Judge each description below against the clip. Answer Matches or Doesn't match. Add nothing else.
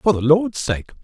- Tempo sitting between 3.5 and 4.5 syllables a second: Matches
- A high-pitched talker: Doesn't match